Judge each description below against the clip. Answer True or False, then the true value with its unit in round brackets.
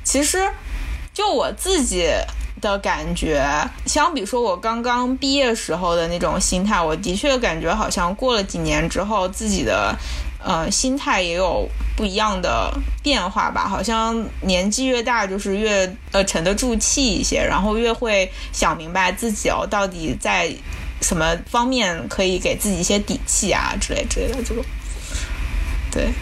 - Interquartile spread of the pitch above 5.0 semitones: True (5.5 semitones)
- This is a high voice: True (200 Hz)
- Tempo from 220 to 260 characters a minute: True (235 characters per minute)